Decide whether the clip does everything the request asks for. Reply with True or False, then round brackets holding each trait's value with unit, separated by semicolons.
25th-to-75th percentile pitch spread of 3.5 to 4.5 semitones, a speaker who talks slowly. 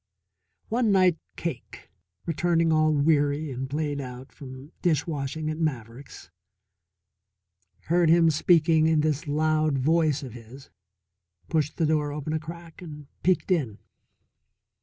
False (2.5 semitones; 130 wpm)